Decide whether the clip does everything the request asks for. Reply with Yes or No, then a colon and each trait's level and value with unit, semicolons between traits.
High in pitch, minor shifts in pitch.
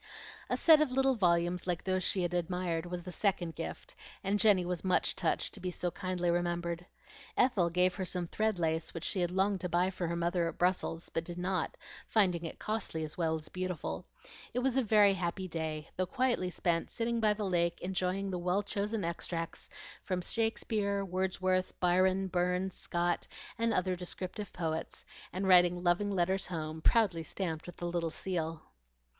No: medium, 180 Hz; narrow, 2.1 semitones